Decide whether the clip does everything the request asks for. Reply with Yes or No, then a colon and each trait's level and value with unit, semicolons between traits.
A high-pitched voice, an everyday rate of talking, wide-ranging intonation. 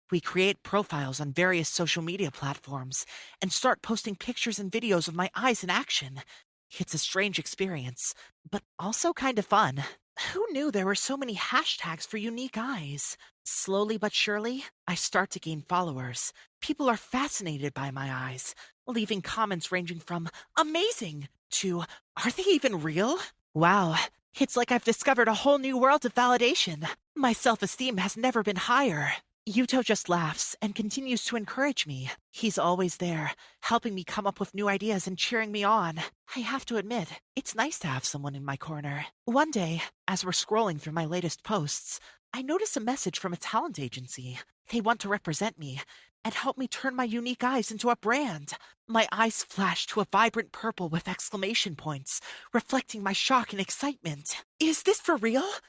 Yes: high, 205 Hz; average, 180 wpm; wide, 6.1 semitones